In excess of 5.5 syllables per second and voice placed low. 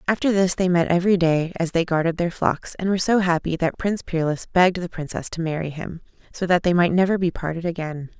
No: 6.0 syllables/s; medium, 175 Hz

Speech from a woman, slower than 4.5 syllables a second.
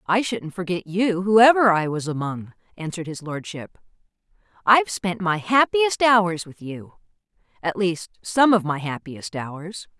Yes: female; 4.3 syllables/s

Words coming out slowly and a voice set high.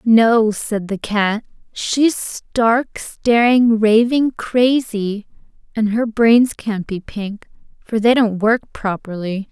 Yes: slow, 125 wpm; high, 220 Hz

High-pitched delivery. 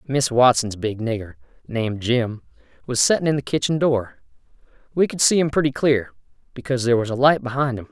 No: low, 130 Hz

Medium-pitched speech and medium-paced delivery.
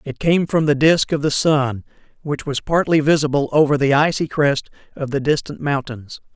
Yes: medium, 145 Hz; average, 190 wpm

